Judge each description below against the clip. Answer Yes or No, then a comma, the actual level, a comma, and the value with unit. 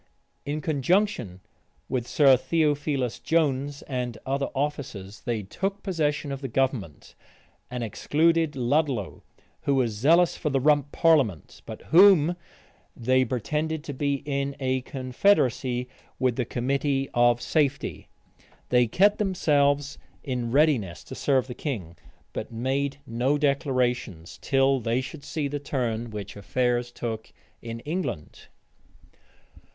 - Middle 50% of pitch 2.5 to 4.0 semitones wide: Yes, average, 3.4 semitones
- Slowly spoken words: Yes, slow, 125 wpm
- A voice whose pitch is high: No, low, 135 Hz